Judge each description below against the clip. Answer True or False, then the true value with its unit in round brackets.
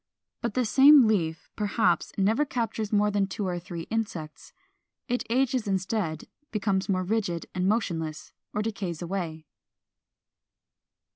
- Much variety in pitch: False (4.2 semitones)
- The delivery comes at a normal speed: False (130 wpm)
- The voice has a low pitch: False (200 Hz)